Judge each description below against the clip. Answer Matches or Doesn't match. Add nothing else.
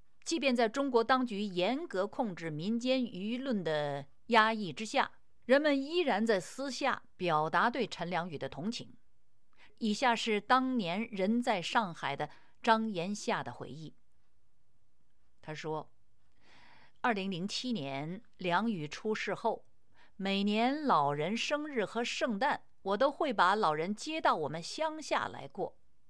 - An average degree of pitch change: Doesn't match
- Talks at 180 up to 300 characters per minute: Matches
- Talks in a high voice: Matches